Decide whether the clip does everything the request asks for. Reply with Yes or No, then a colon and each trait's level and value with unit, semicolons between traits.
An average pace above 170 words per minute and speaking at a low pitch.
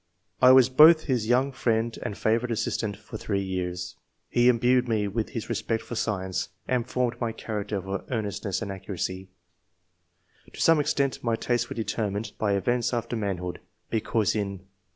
No: average, 165 wpm; low, 110 Hz